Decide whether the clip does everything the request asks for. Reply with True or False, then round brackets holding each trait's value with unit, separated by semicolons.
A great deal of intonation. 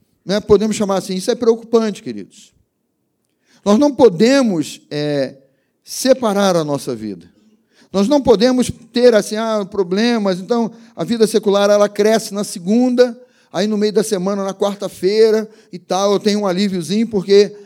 False (2.8 semitones)